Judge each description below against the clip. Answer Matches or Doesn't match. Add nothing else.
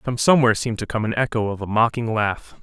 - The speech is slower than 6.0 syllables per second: Doesn't match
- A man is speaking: Matches